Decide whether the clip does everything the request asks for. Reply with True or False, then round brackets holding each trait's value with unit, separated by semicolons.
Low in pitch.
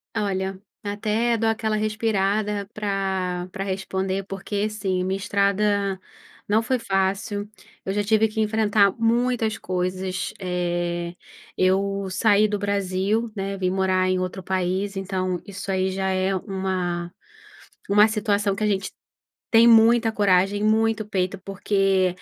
False (195 Hz)